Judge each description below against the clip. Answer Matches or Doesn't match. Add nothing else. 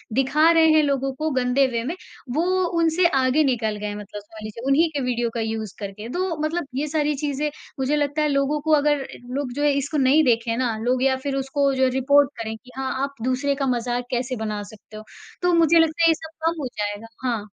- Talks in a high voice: Matches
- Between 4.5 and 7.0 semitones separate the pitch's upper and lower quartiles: Doesn't match